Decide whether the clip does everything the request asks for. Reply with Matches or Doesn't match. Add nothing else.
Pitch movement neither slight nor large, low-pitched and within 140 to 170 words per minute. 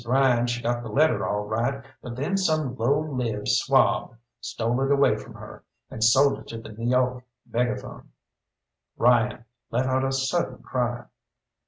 Doesn't match